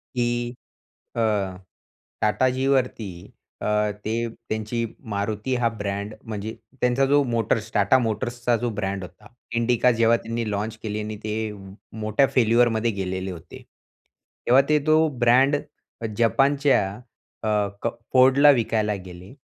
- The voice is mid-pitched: No, low, 115 Hz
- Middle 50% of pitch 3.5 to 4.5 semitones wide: No, average, 2.9 semitones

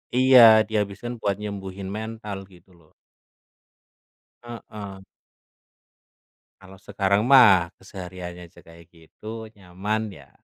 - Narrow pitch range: No, average, 3.0 semitones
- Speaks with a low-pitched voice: Yes, low, 100 Hz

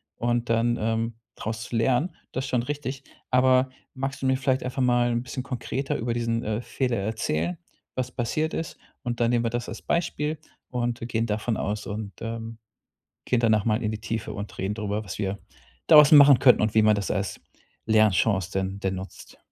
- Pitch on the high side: No, low, 115 Hz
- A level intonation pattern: No, average, 3.0 semitones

